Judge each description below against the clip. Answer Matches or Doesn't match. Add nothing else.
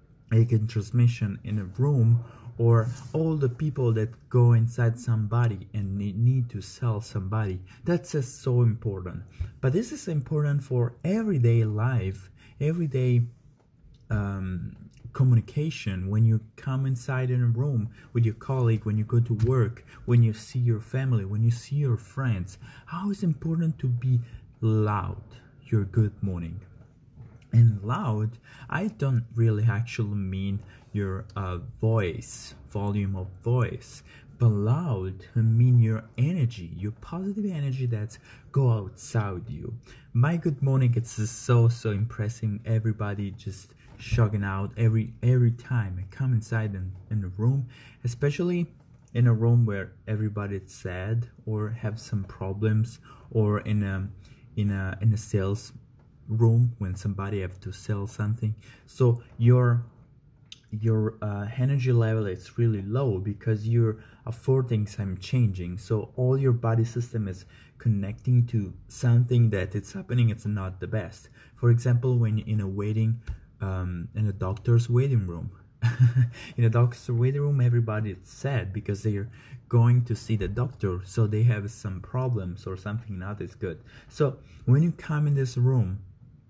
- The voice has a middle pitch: Doesn't match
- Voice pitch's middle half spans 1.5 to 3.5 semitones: Matches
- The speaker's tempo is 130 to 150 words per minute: Matches